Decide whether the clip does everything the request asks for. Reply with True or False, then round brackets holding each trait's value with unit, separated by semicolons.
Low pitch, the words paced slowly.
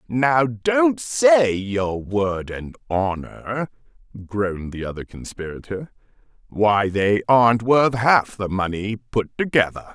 True (115 Hz; 120 wpm)